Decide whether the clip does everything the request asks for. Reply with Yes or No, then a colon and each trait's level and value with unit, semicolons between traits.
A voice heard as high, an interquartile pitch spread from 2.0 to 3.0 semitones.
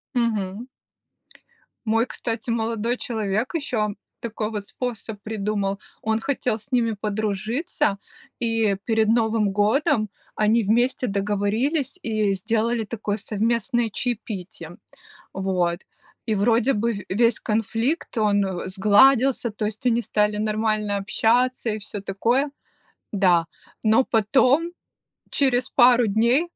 Yes: high, 220 Hz; narrow, 2.6 semitones